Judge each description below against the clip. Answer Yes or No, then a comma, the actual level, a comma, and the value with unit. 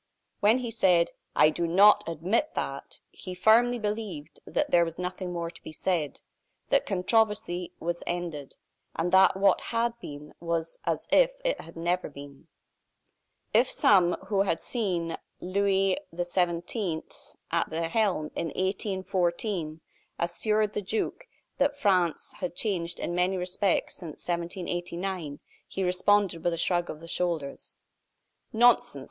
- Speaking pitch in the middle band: Yes, medium, 180 Hz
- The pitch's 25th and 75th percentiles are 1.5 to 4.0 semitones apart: Yes, average, 3.3 semitones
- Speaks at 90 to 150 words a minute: Yes, average, 140 wpm